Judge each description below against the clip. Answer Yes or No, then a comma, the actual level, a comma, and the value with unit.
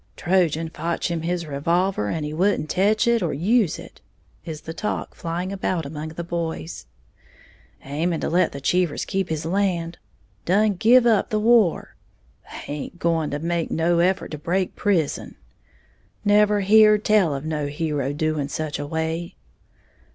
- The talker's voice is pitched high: No, medium, 170 Hz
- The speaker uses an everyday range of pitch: Yes, average, 3.6 semitones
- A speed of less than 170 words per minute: Yes, average, 160 wpm